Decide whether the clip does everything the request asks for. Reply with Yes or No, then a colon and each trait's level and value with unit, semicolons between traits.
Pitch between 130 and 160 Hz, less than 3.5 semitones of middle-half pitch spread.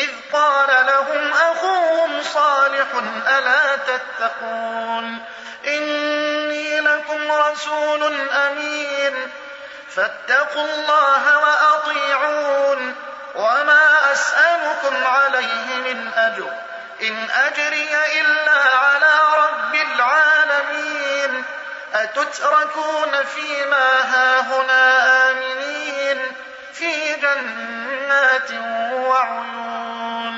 No: very high, 285 Hz; narrow, 2.6 semitones